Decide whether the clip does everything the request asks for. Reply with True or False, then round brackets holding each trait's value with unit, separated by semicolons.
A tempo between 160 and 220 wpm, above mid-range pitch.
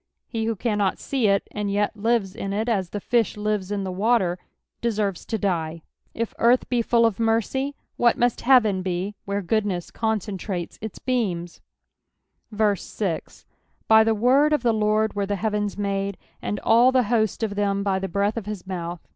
True (180 wpm; 210 Hz)